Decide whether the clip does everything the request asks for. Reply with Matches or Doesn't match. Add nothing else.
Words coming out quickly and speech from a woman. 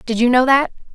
Matches